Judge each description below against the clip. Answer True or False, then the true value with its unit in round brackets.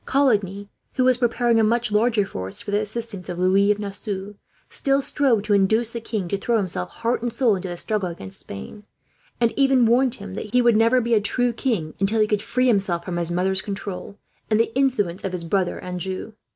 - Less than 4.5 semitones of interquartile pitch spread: True (3.7 semitones)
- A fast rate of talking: True (215 wpm)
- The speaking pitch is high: True (210 Hz)